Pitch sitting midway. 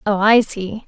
No: high, 205 Hz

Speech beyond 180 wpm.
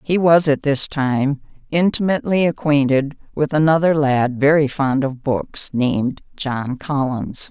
No: slow, 135 wpm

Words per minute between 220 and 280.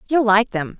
Yes: fast, 225 wpm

